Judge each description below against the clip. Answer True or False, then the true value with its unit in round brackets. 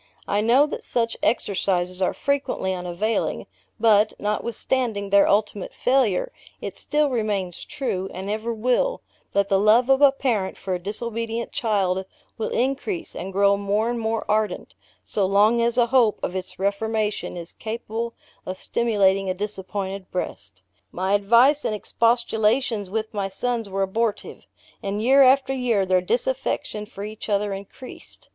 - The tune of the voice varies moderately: True (3.2 semitones)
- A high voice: True (215 Hz)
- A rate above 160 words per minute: False (150 wpm)